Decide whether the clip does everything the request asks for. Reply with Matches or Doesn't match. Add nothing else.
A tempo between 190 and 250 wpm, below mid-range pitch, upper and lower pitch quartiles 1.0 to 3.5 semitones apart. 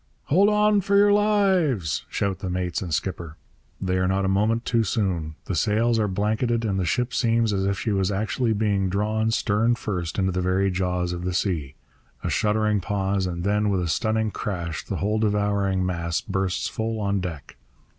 Matches